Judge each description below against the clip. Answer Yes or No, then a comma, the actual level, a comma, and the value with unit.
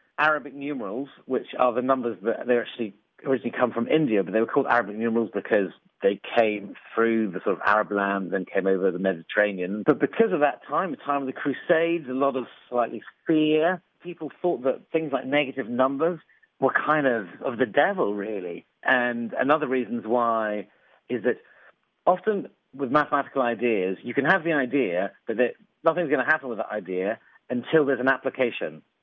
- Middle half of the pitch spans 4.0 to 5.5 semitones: Yes, average, 4.8 semitones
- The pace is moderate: Yes, average, 185 wpm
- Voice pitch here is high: No, low, 125 Hz